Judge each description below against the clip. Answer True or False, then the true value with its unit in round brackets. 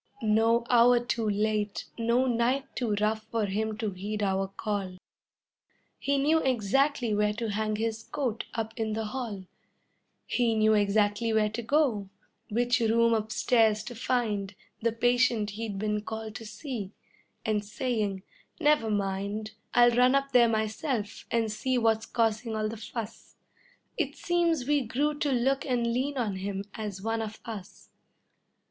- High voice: True (225 Hz)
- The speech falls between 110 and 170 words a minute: True (155 wpm)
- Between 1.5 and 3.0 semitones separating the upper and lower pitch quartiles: True (2.5 semitones)